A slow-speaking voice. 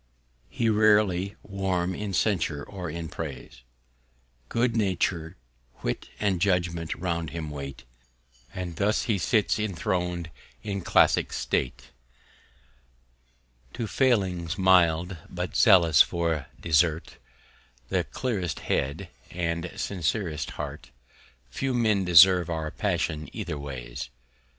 Yes: slow, 110 wpm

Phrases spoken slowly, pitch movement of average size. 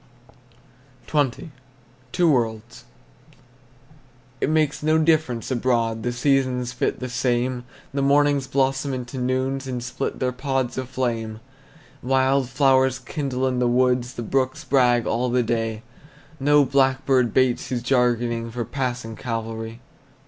No: slow, 130 wpm; narrow, 2.0 semitones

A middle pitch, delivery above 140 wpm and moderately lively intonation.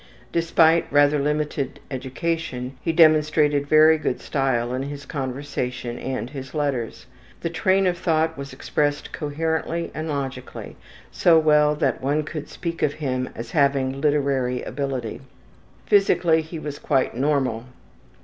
No: medium, 145 Hz; slow, 135 wpm; average, 3.1 semitones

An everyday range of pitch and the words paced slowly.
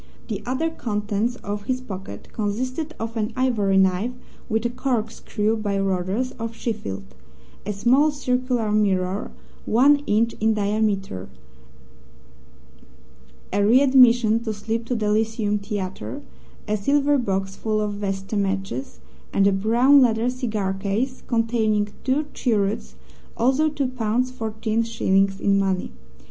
Yes: average, 3.6 semitones; slow, 130 wpm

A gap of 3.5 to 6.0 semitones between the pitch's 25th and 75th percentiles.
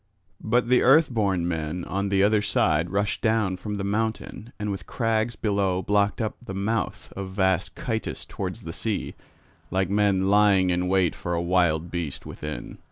No: average, 3.1 semitones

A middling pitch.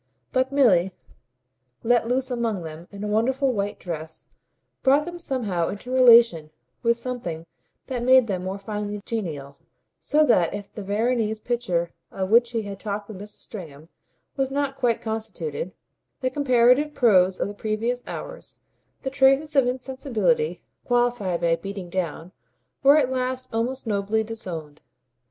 No: high, 225 Hz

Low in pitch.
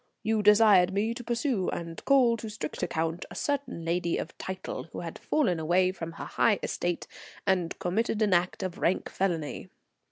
No: medium, 185 Hz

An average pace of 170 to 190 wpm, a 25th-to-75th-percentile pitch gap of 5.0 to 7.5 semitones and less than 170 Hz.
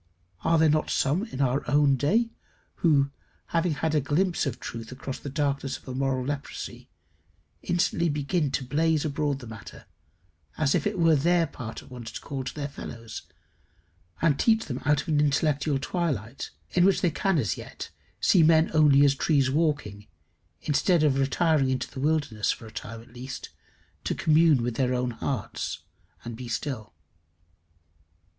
No: average, 175 wpm; average, 3.6 semitones; medium, 140 Hz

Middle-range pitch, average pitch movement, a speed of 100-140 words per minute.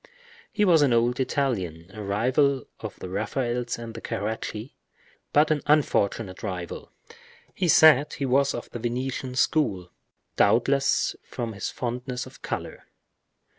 No: low, 125 Hz; average, 4.4 semitones; slow, 135 wpm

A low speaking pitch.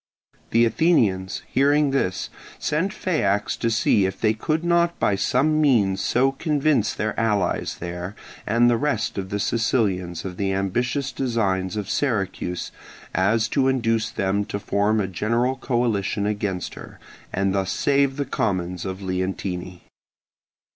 Yes: low, 110 Hz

